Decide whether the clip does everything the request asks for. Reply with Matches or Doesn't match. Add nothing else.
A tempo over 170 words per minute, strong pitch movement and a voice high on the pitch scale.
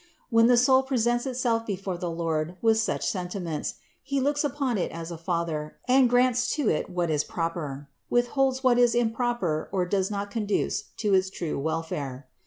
Matches